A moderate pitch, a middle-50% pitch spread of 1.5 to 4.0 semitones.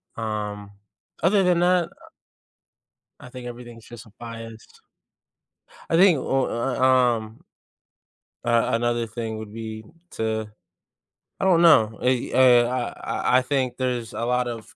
No: low, 120 Hz; narrow, 2.6 semitones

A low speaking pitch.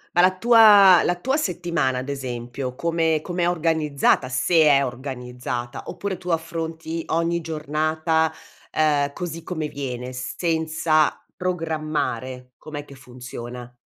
No: medium, 155 Hz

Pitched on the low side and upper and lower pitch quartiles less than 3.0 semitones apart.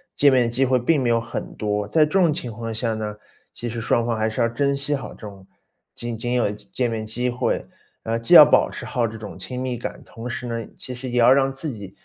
Yes: low, 120 Hz; narrow, 2.4 semitones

